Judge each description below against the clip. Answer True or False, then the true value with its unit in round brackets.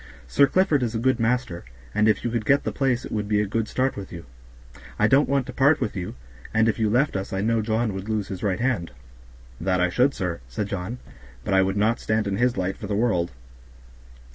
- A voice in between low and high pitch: False (110 Hz)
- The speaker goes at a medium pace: False (245 wpm)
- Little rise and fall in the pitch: False (4.3 semitones)